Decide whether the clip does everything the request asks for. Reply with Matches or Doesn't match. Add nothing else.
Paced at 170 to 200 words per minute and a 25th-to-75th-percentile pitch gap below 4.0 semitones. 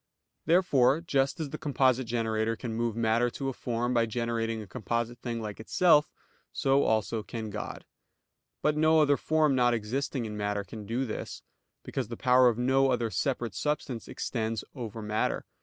Matches